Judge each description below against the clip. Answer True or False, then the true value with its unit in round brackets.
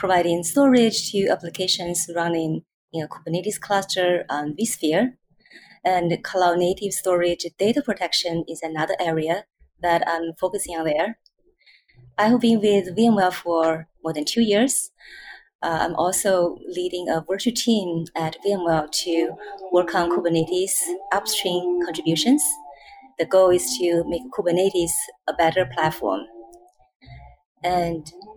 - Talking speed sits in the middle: False (125 wpm)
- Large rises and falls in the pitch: False (3.3 semitones)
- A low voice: False (175 Hz)